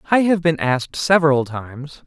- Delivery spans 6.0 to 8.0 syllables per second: No, 5.4 syllables/s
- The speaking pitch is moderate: Yes, medium, 150 Hz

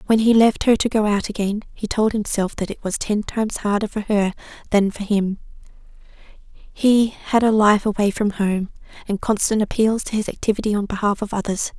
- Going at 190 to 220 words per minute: Yes, average, 200 wpm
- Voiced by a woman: Yes, female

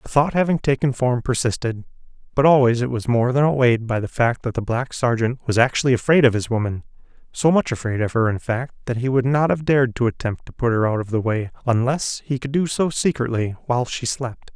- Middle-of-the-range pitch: No, low, 125 Hz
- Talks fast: Yes, fast, 235 wpm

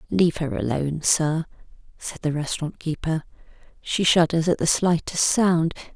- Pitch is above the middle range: No, medium, 165 Hz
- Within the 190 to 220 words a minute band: No, average, 140 wpm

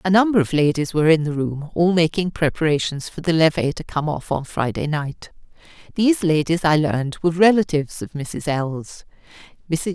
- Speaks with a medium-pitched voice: Yes, medium, 160 Hz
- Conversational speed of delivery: Yes, average, 175 wpm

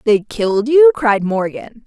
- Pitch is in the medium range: No, high, 230 Hz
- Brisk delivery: No, average, 160 wpm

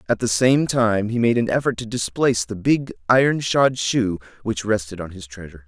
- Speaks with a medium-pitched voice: No, low, 110 Hz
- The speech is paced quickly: Yes, fast, 210 wpm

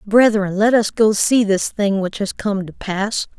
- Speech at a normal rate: No, fast, 215 wpm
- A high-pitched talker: Yes, high, 205 Hz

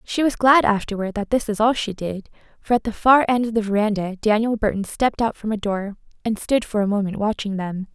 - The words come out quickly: Yes, fast, 240 wpm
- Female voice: Yes, female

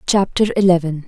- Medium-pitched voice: Yes, medium, 180 Hz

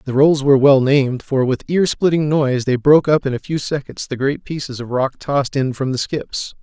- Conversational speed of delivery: No, fast, 245 wpm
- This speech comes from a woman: No, male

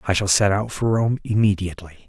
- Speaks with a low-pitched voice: Yes, low, 100 Hz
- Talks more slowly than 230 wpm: Yes, average, 200 wpm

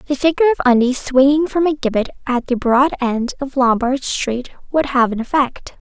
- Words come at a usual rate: Yes, average, 195 wpm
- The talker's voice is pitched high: Yes, very high, 265 Hz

